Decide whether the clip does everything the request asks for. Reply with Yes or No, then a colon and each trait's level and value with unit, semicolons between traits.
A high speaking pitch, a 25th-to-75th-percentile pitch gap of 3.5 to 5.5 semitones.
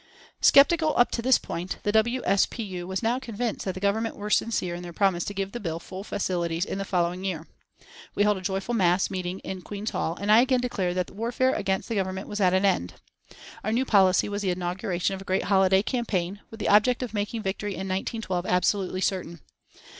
No: high, 195 Hz; average, 3.0 semitones